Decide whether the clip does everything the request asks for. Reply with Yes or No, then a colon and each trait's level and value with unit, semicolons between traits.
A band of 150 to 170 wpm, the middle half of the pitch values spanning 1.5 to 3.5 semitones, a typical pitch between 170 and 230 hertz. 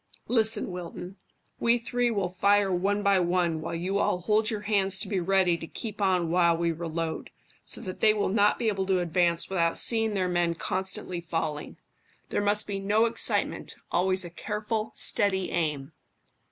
No: average, 180 wpm; average, 3.2 semitones; high, 190 Hz